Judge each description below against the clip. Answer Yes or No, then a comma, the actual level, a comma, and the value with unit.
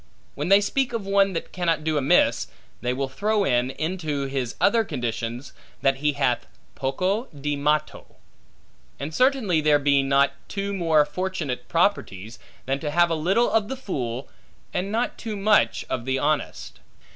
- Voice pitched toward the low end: No, medium, 155 Hz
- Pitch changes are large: Yes, wide, 6.4 semitones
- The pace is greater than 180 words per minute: No, average, 165 wpm